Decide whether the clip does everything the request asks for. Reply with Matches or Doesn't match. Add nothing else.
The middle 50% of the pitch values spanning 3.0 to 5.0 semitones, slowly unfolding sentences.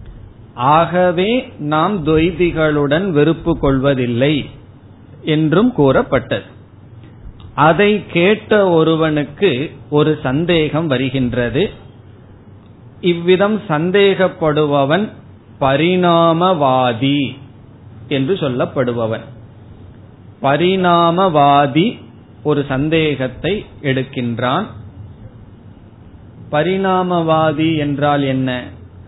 Doesn't match